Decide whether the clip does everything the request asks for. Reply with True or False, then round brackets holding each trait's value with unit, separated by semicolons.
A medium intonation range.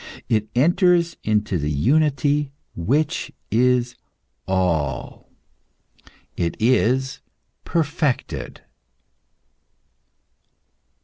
False (6.4 semitones)